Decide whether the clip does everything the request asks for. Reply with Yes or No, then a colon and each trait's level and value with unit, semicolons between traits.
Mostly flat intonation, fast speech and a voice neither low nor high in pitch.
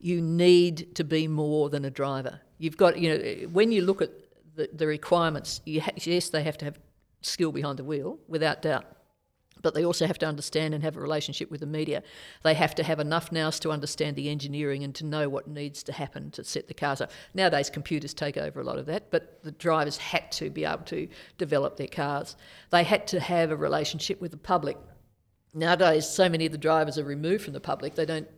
Yes: narrow, 2.1 semitones; fast, 230 wpm; medium, 155 Hz